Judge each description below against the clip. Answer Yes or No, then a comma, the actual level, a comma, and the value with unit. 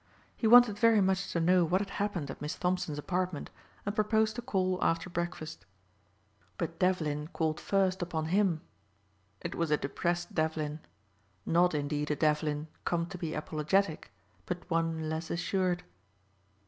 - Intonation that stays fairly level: No, average, 3.2 semitones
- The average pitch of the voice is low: No, medium, 175 Hz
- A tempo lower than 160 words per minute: Yes, average, 150 wpm